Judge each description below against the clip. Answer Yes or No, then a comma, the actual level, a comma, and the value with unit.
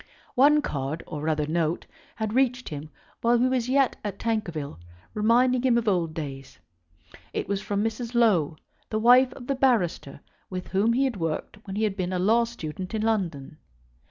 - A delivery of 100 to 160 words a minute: No, average, 185 wpm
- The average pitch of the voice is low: No, high, 210 Hz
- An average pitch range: No, wide, 6.6 semitones